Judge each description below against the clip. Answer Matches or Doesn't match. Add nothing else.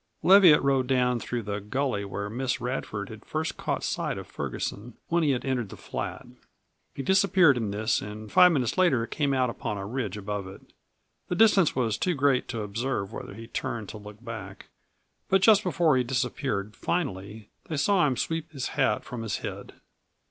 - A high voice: Doesn't match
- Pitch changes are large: Matches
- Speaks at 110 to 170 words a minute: Doesn't match